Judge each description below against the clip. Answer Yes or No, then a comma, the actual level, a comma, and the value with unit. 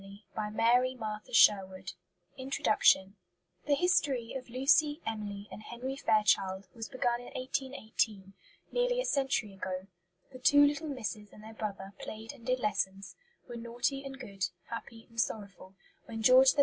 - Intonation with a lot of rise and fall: No, average, 4.2 semitones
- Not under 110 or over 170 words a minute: Yes, average, 150 wpm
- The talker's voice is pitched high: Yes, high, 230 Hz